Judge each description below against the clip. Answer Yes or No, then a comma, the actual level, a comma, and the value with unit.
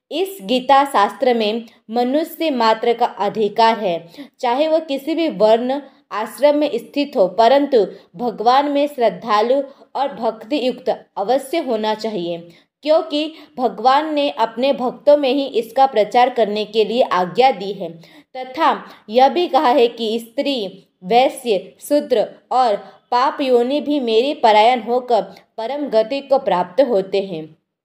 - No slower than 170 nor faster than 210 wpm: No, average, 140 wpm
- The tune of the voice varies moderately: Yes, average, 4.4 semitones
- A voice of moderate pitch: No, high, 245 Hz